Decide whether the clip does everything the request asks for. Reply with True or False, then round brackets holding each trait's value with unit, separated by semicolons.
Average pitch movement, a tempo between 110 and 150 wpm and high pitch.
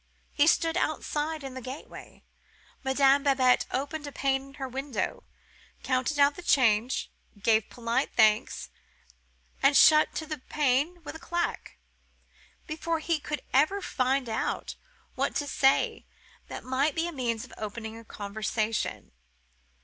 True (3.7 semitones; 140 wpm; 270 Hz)